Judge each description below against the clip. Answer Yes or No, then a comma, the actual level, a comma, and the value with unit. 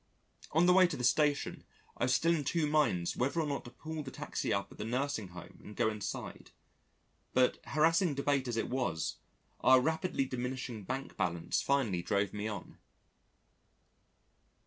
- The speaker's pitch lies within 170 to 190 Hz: No, low, 130 Hz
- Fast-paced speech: No, average, 170 wpm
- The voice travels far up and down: Yes, wide, 5.7 semitones